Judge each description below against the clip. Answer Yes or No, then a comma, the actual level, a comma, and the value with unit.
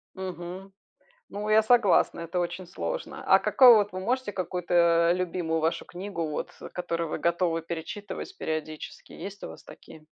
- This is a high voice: No, medium, 180 Hz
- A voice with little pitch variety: No, average, 3.2 semitones